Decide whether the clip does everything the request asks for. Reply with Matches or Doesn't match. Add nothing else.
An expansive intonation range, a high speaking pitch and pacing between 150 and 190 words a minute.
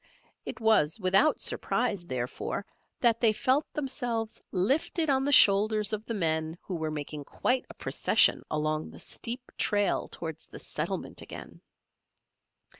Doesn't match